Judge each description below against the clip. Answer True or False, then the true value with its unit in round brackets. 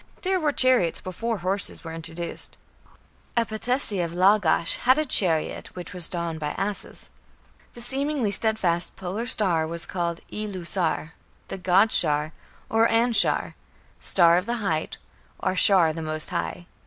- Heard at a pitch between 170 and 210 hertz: True (185 Hz)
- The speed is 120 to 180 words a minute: True (150 wpm)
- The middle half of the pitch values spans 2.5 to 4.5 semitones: False (5.0 semitones)